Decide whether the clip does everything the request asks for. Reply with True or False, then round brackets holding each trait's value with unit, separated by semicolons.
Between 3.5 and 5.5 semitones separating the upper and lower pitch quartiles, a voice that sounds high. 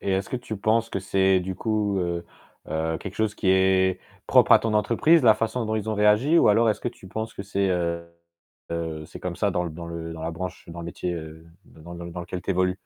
False (3.9 semitones; 95 Hz)